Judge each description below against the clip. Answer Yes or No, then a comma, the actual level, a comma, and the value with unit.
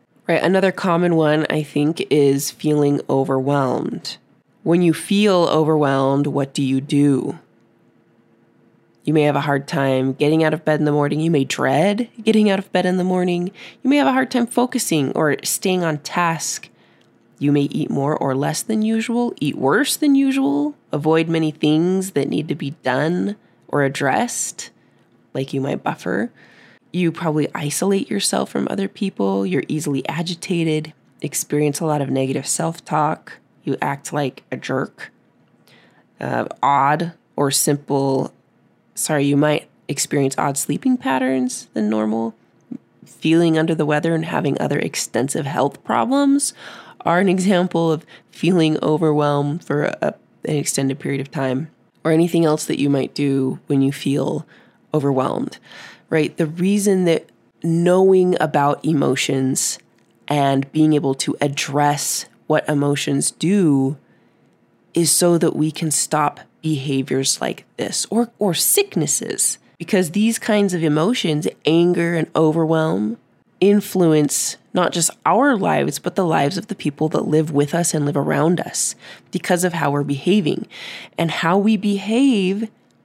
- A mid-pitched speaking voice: Yes, medium, 155 Hz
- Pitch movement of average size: Yes, average, 4.1 semitones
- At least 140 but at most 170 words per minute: Yes, average, 150 wpm